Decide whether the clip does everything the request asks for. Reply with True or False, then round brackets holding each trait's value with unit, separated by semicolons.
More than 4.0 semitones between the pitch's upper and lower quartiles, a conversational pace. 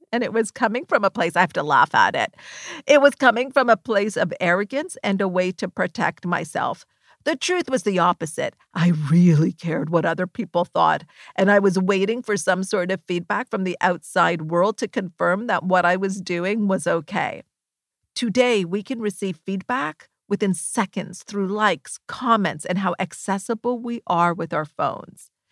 True (4.5 semitones; 185 wpm)